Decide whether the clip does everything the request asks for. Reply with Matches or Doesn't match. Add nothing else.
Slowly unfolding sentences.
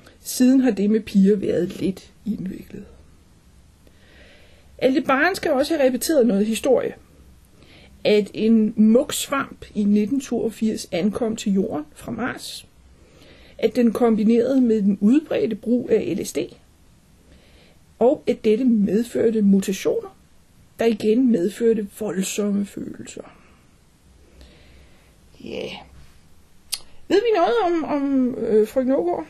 Matches